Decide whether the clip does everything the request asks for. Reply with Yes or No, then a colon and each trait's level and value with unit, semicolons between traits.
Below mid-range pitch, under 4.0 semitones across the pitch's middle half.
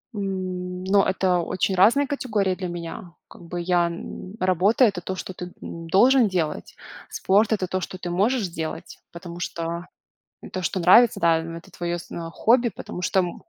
No: medium, 185 Hz; narrow, 2.4 semitones